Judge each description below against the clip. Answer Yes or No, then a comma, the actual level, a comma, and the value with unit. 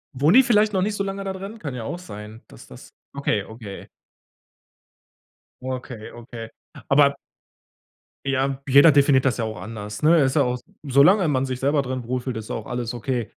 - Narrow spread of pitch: No, average, 4.3 semitones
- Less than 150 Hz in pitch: Yes, low, 135 Hz